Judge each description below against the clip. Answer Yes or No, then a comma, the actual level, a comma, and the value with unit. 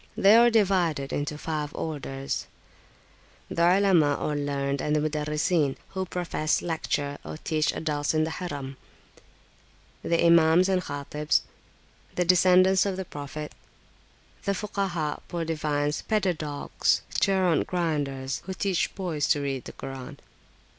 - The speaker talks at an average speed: No, slow, 130 wpm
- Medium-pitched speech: Yes, medium, 155 Hz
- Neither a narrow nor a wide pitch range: Yes, average, 3.9 semitones